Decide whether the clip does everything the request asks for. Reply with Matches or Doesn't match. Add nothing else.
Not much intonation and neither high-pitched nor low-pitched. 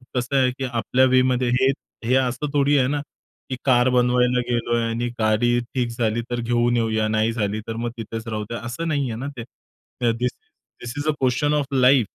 Doesn't match